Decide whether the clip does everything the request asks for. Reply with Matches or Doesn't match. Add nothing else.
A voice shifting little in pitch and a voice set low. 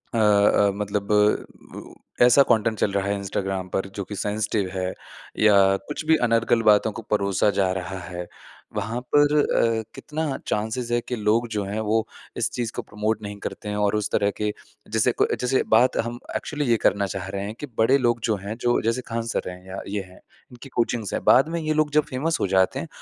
Doesn't match